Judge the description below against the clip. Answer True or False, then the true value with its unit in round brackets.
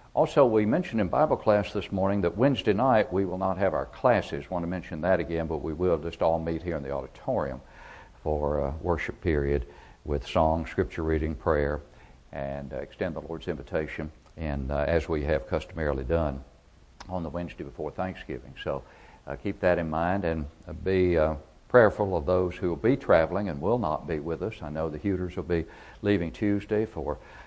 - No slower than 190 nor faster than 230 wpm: True (195 wpm)